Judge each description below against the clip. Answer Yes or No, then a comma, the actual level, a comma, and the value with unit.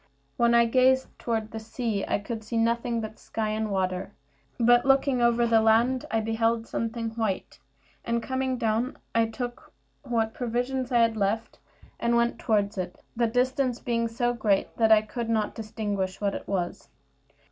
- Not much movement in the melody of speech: Yes, narrow, 1.8 semitones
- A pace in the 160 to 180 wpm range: Yes, average, 170 wpm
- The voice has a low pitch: No, high, 230 Hz